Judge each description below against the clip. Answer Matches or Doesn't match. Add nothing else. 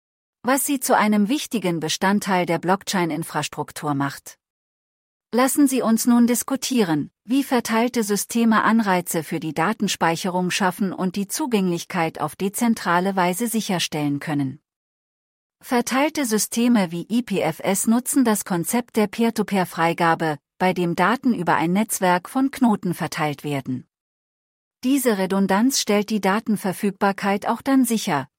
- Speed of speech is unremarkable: Doesn't match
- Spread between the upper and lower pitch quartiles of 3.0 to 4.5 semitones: Doesn't match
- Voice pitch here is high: Matches